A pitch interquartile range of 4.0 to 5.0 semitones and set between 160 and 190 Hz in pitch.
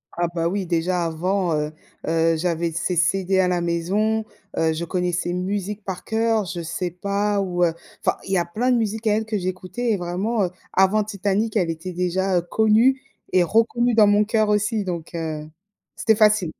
No: average, 3.6 semitones; medium, 185 Hz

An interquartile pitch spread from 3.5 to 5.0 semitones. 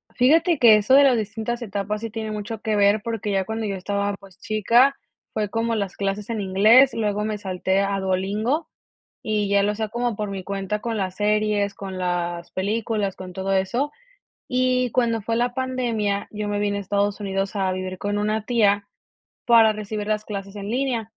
No: narrow, 2.4 semitones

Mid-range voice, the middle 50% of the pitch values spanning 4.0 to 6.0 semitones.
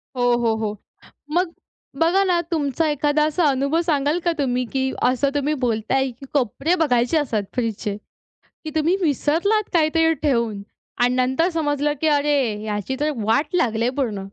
No: very high, 285 Hz; average, 4.5 semitones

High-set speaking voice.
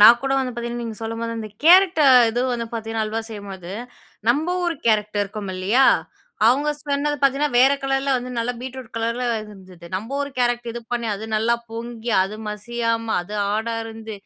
Yes: high, 230 Hz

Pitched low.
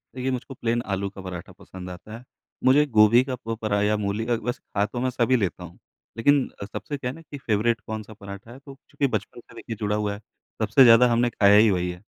Yes: low, 110 Hz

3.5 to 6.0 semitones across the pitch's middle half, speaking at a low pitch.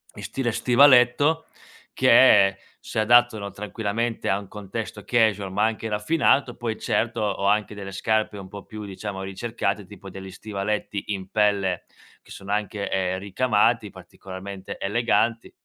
No: average, 2.8 semitones; low, 105 Hz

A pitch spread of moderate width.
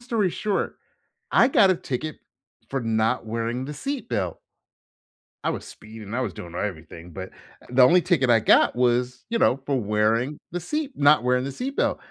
No: wide, 6.9 semitones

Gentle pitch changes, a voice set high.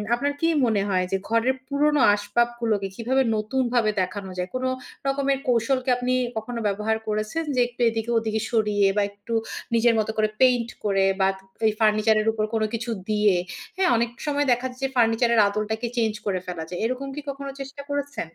No: average, 3.2 semitones; high, 230 Hz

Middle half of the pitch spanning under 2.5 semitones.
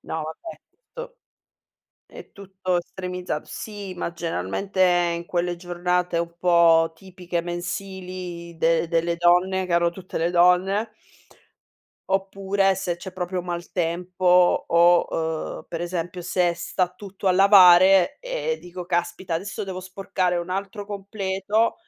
Yes: narrow, 1.9 semitones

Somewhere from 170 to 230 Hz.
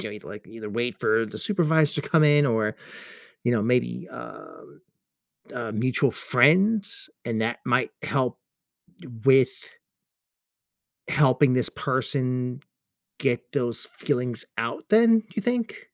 No: low, 125 Hz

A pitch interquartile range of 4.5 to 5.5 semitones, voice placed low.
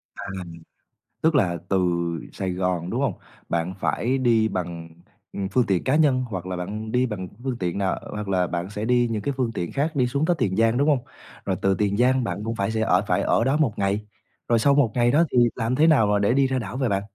Yes: average, 4.8 semitones; low, 110 Hz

